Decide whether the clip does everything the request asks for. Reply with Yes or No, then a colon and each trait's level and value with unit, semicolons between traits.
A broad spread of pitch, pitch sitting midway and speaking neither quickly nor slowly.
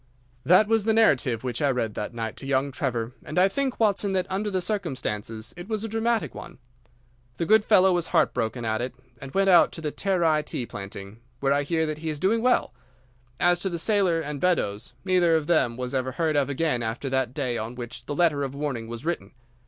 No: wide, 6.9 semitones; medium, 150 Hz; fast, 225 wpm